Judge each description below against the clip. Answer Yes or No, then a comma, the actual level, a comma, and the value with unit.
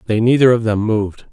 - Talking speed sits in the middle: No, fast, 225 wpm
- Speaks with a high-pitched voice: No, low, 110 Hz